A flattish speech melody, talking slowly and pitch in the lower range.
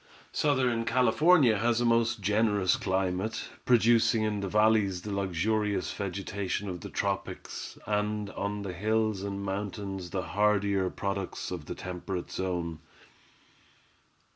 Yes: narrow, 2.3 semitones; slow, 125 wpm; low, 100 Hz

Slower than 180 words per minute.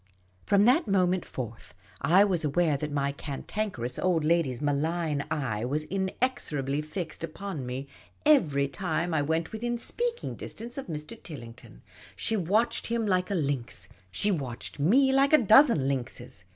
Yes: average, 160 wpm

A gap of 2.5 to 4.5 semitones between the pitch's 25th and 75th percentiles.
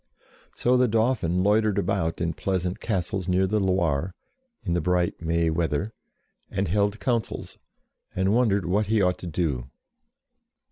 Yes: average, 3.6 semitones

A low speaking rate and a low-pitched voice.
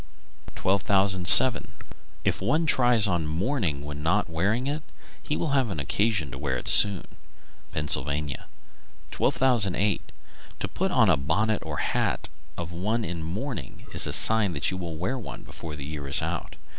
No: average, 160 wpm; very low, 95 Hz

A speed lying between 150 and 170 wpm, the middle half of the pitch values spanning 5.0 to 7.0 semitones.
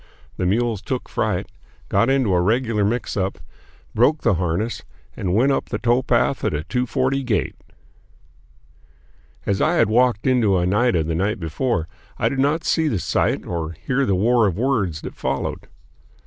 Yes: average, 165 wpm; wide, 5.5 semitones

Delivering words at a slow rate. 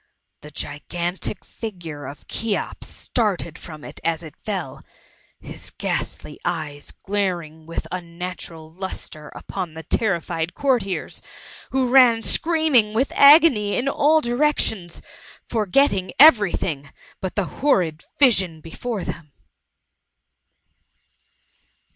Yes: slow, 110 wpm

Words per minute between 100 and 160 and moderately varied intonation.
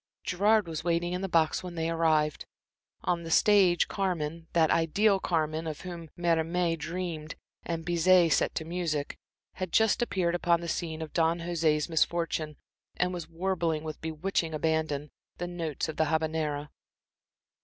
No: average, 155 wpm; narrow, 1.8 semitones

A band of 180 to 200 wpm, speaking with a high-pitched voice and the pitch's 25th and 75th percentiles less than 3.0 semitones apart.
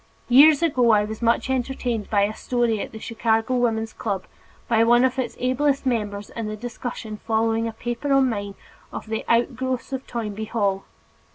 Yes: average, 185 wpm; high, 230 Hz; narrow, 2.6 semitones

